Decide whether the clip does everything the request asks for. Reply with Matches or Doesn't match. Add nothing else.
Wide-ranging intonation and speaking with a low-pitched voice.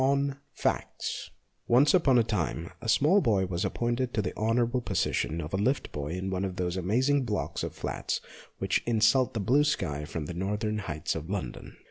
Matches